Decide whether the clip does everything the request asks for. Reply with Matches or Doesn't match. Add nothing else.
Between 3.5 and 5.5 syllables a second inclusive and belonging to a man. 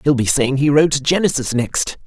Matches